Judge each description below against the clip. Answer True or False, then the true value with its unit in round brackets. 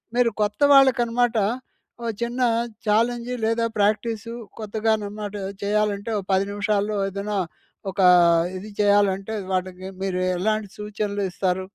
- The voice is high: True (210 Hz)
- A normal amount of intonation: False (2.2 semitones)